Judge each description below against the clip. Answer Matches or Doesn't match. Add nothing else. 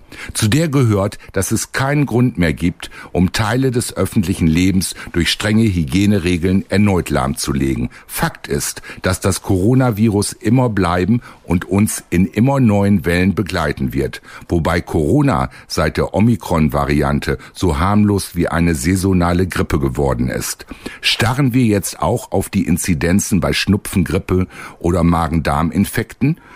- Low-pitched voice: Matches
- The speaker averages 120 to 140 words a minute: Matches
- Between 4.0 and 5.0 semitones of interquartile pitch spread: Matches